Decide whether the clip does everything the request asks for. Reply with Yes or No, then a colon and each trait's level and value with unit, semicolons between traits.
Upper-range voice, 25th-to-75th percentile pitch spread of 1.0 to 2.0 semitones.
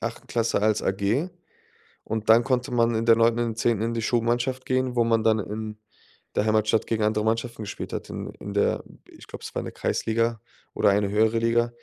No: low, 115 Hz; narrow, 1.5 semitones